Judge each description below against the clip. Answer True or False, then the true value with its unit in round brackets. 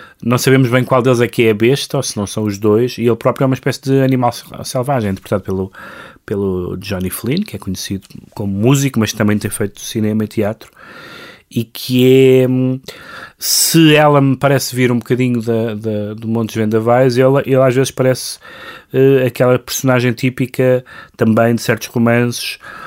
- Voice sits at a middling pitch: False (125 Hz)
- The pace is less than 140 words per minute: False (185 wpm)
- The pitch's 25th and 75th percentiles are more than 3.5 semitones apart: False (3.2 semitones)